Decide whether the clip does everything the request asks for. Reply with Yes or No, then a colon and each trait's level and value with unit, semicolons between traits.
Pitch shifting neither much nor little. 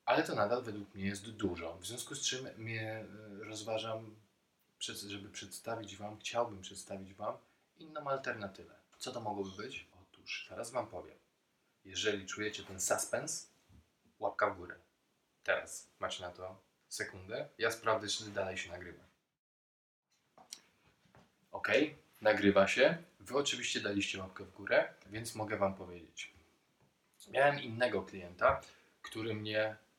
No: narrow, 2.3 semitones